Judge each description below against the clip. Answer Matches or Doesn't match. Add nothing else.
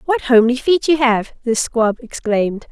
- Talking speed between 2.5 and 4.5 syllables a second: Doesn't match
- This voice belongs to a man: Doesn't match